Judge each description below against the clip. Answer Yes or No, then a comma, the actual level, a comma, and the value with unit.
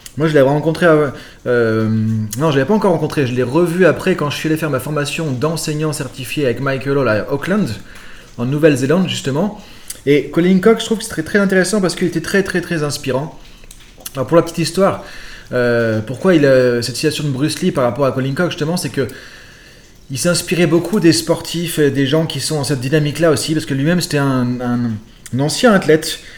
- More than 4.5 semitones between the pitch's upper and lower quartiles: No, average, 4.2 semitones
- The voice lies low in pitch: No, medium, 150 Hz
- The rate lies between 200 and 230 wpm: Yes, fast, 220 wpm